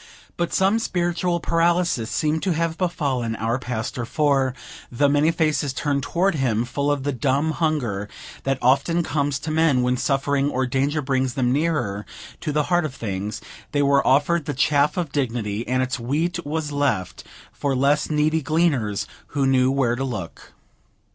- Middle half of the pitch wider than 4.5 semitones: No, average, 3.8 semitones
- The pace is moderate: Yes, average, 170 wpm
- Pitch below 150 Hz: Yes, medium, 140 Hz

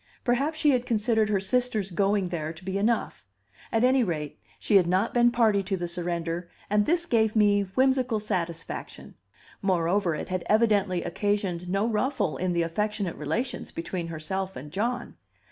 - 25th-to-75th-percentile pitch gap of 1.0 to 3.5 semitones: No, average, 4.6 semitones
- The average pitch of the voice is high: Yes, high, 200 Hz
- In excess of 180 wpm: No, average, 165 wpm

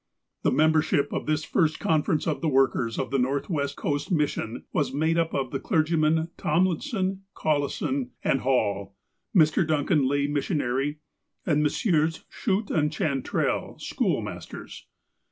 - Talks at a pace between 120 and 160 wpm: Yes, slow, 135 wpm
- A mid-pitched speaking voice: Yes, medium, 150 Hz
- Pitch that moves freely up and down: No, narrow, 2.6 semitones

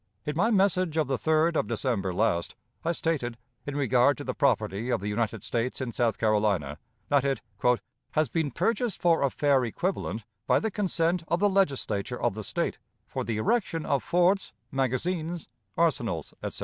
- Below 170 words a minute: No, average, 175 wpm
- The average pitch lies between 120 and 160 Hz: Yes, medium, 140 Hz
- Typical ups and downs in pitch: No, wide, 6.8 semitones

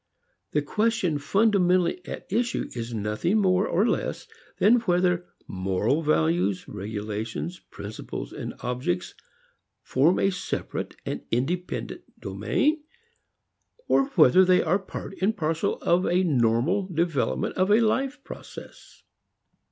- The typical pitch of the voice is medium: Yes, medium, 175 Hz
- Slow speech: Yes, slow, 120 wpm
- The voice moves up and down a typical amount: No, wide, 8.7 semitones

